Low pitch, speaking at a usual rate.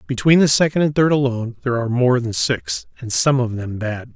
No: low, 125 Hz; fast, 230 wpm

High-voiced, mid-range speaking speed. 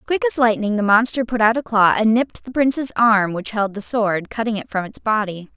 No: high, 225 Hz; fast, 250 wpm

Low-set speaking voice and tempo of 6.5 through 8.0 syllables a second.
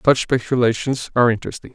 Yes: low, 125 Hz; 6.8 syllables/s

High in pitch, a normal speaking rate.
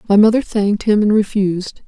Yes: high, 205 Hz; average, 190 wpm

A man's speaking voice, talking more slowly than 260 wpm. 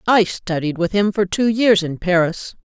No: female; fast, 205 wpm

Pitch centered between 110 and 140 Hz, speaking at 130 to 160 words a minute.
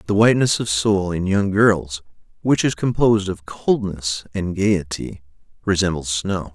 No: very low, 95 Hz; average, 145 wpm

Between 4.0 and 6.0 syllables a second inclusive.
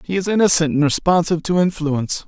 No: 6.5 syllables/s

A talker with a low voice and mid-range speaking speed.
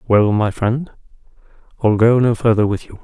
Yes: low, 110 Hz; average, 180 wpm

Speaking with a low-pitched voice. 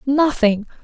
No: very high, 255 Hz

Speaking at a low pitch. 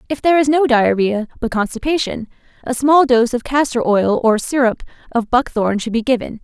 No: high, 245 Hz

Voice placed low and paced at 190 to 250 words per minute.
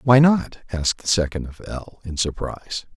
No: low, 100 Hz; average, 180 wpm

